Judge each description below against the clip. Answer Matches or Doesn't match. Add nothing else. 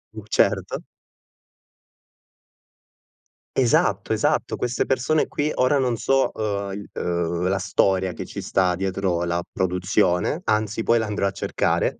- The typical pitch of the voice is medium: Doesn't match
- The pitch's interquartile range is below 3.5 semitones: Doesn't match